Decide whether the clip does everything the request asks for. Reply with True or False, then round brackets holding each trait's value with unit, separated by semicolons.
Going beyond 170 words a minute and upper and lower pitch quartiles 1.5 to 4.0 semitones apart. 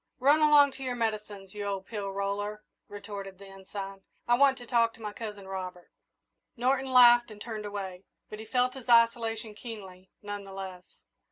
True (180 wpm; 3.5 semitones)